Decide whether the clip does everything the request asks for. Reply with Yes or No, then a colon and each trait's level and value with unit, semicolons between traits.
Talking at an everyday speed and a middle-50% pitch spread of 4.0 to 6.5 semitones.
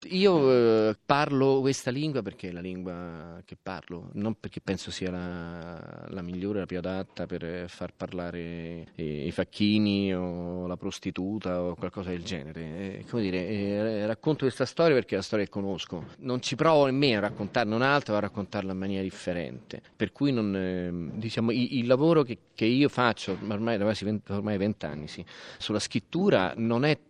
No: fast, 185 wpm; average, 4.6 semitones